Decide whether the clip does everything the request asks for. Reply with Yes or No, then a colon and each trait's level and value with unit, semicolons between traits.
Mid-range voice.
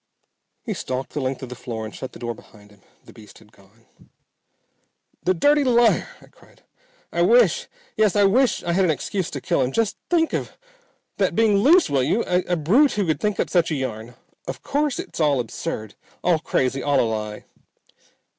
Yes: medium, 155 Hz